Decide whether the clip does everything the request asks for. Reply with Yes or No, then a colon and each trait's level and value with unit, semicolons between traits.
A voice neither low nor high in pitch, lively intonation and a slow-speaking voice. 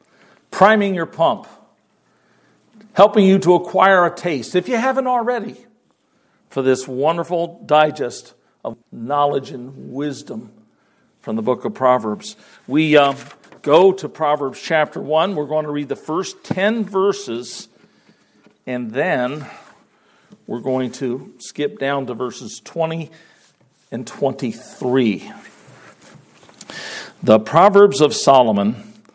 Yes: medium, 155 Hz; wide, 6.3 semitones; slow, 115 wpm